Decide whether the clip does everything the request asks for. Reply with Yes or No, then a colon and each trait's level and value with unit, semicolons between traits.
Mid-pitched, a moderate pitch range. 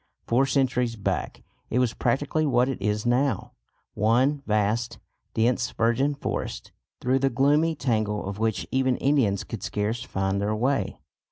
No: low, 120 Hz; average, 3.8 semitones